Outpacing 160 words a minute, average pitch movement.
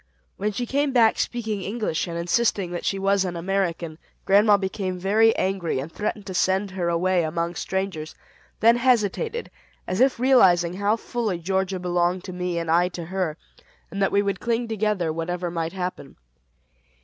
Yes: average, 175 wpm; average, 3.3 semitones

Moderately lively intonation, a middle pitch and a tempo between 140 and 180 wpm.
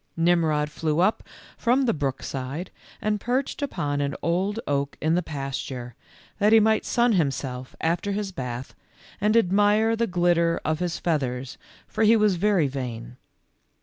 No: wide, 7.0 semitones; medium, 170 Hz; average, 155 wpm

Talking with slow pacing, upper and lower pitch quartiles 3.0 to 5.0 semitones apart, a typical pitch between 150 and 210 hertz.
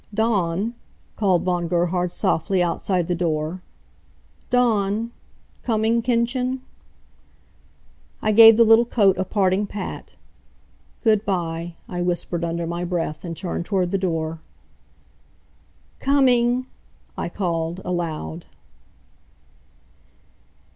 Yes: slow, 100 wpm; average, 4.5 semitones; medium, 185 Hz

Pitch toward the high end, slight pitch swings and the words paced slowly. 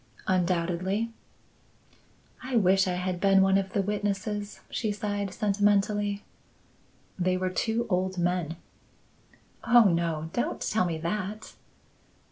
Yes: high, 195 Hz; narrow, 2.3 semitones; slow, 115 wpm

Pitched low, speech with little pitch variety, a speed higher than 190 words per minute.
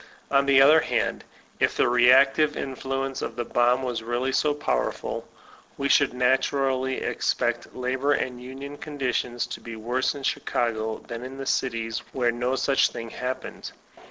No: low, 130 Hz; narrow, 2.0 semitones; average, 160 wpm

